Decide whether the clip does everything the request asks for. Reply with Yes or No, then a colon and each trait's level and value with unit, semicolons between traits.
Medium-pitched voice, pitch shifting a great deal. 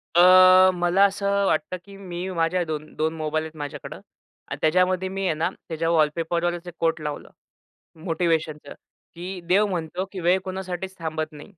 No: medium, 170 Hz; average, 2.7 semitones